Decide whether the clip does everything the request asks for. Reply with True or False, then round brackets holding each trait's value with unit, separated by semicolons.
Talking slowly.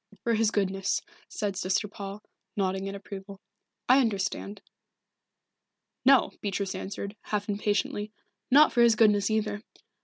True (125 wpm)